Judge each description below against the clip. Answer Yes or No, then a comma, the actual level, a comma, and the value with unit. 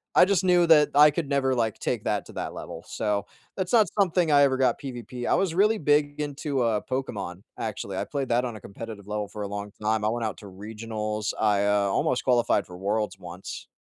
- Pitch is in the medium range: No, low, 115 Hz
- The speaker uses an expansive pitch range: Yes, wide, 5.7 semitones